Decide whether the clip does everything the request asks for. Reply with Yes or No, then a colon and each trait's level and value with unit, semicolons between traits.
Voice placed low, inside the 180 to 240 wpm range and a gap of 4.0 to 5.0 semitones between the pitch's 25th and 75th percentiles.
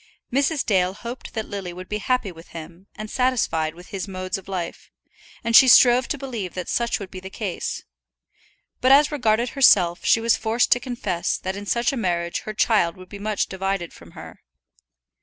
No: high, 205 Hz; average, 195 wpm; average, 4.6 semitones